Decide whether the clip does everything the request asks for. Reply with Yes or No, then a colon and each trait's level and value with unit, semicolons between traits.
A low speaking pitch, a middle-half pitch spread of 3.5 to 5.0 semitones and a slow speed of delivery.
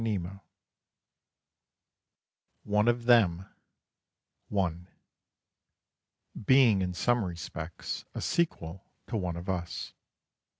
Yes: very low, 95 Hz; average, 4.7 semitones; slow, 85 wpm